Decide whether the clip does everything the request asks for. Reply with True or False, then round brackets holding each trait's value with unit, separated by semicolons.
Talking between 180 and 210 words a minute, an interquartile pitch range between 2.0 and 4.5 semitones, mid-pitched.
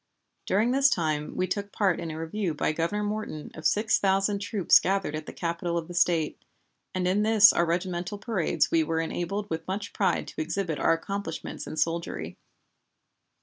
True (190 wpm; 3.8 semitones; 180 Hz)